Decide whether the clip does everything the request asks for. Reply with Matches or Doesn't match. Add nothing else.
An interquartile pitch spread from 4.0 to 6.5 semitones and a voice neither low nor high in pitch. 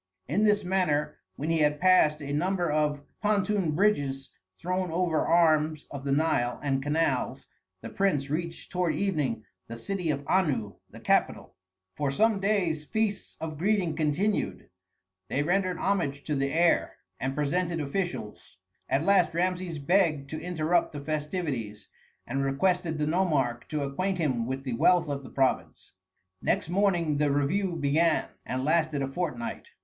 Matches